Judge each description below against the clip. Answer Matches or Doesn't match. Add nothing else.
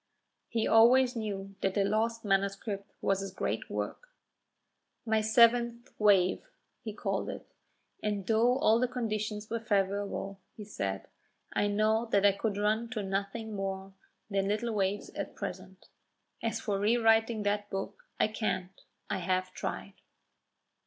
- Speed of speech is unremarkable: Matches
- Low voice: Doesn't match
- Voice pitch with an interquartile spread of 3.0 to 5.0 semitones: Doesn't match